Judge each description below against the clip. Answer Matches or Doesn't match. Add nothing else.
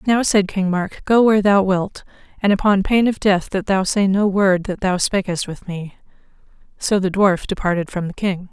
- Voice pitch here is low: Doesn't match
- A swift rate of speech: Matches